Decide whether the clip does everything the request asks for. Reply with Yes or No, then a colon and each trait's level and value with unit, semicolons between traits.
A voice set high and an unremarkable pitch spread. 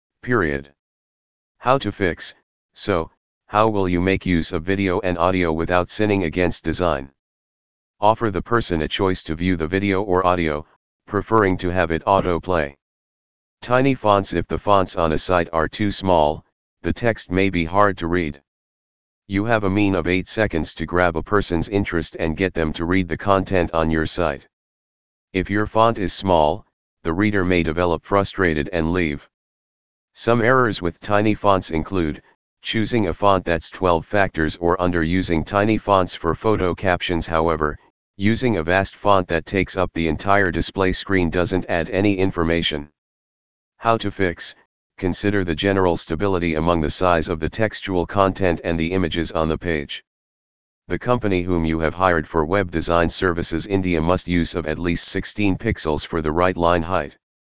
No: very low, 90 Hz; average, 3.2 semitones